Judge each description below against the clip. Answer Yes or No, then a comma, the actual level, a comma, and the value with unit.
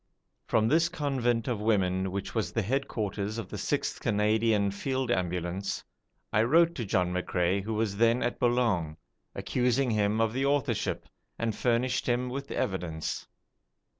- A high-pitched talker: No, low, 110 Hz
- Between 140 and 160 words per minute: Yes, average, 150 wpm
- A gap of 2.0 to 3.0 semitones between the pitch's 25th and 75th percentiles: No, average, 4.0 semitones